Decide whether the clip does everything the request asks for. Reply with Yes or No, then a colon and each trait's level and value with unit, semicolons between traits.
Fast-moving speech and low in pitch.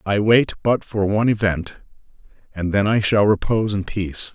No: average, 180 wpm; low, 100 Hz